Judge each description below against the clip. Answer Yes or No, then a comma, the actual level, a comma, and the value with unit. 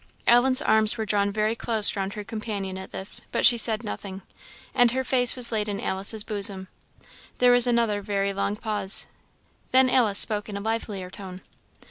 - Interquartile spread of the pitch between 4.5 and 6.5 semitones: No, average, 2.9 semitones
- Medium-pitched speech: No, high, 215 Hz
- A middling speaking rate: Yes, average, 180 wpm